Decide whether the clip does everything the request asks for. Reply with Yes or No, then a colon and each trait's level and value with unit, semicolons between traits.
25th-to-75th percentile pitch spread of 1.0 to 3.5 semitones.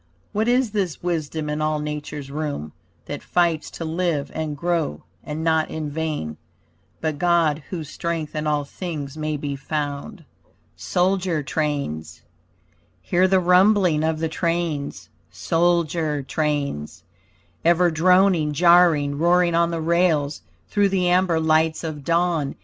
Yes: average, 2.8 semitones